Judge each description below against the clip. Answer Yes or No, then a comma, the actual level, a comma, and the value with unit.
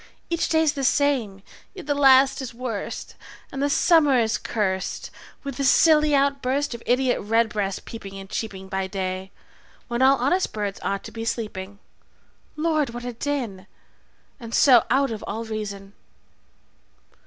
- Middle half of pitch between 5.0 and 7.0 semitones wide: Yes, wide, 5.4 semitones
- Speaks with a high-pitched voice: Yes, high, 240 Hz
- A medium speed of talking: Yes, average, 155 wpm